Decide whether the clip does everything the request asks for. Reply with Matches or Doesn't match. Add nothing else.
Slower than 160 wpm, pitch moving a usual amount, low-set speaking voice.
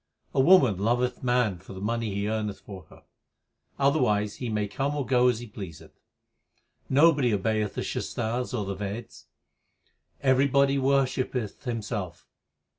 Matches